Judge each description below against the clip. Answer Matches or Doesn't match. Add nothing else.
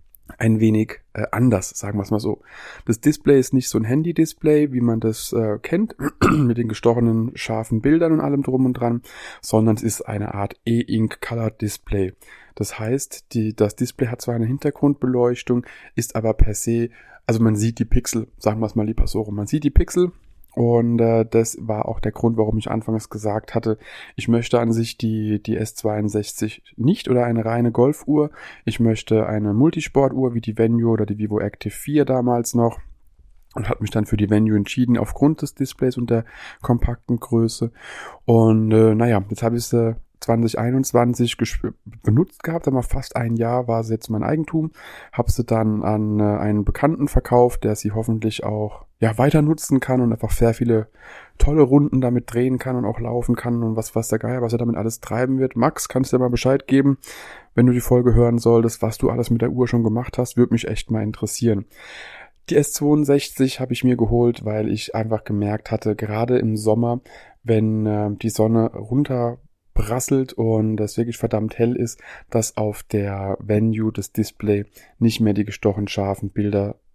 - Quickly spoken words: Matches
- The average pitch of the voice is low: Matches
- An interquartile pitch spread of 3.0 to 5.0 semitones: Doesn't match